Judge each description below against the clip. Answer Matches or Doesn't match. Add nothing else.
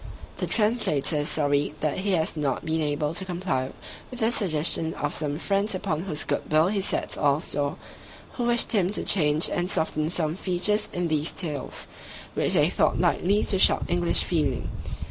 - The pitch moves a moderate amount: Matches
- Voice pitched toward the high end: Doesn't match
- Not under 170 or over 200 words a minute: Matches